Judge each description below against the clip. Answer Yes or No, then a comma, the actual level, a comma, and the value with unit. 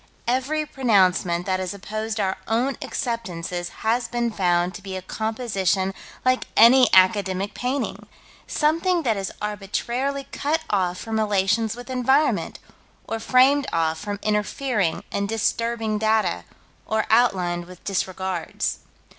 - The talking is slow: Yes, slow, 130 wpm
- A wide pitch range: No, average, 4.5 semitones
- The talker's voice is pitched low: No, high, 215 Hz